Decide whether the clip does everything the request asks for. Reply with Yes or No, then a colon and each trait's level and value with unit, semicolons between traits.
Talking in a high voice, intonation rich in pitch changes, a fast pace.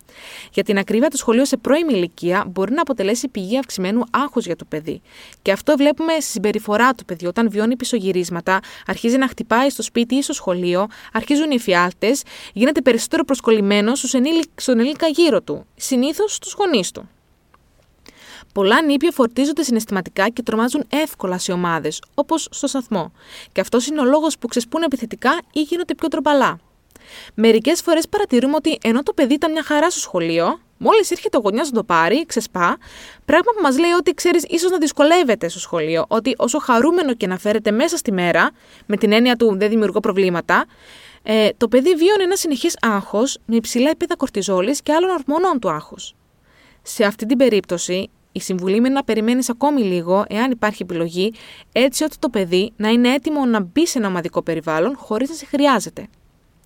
Yes: high, 245 Hz; wide, 6.8 semitones; fast, 175 wpm